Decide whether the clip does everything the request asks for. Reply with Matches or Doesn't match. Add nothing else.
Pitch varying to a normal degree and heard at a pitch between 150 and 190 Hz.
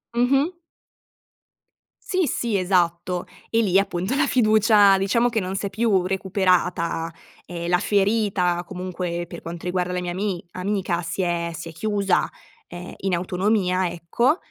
Matches